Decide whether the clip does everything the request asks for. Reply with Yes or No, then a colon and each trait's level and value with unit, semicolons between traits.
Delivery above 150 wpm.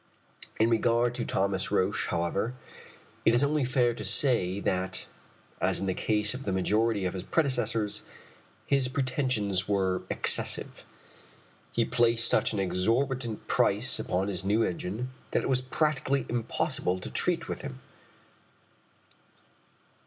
No: average, 140 wpm